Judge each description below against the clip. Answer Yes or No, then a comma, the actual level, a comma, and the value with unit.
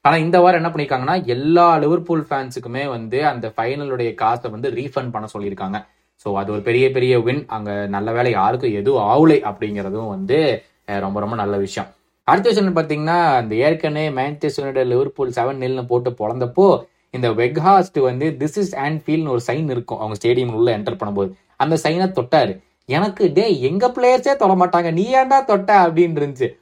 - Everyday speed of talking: No, fast, 165 wpm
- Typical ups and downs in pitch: No, wide, 6.2 semitones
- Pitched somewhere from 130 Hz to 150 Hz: Yes, medium, 140 Hz